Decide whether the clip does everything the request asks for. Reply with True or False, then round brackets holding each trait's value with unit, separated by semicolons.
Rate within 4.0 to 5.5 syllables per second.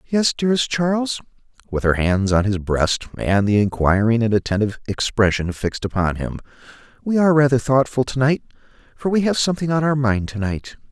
False (5.8 syllables/s)